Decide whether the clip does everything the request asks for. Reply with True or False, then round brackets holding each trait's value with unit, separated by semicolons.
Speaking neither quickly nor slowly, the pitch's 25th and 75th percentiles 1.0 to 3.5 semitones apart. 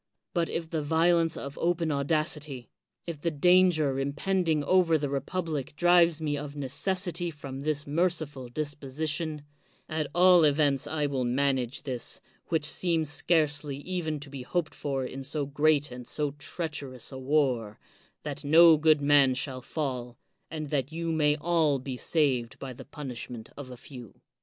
True (155 wpm; 3.0 semitones)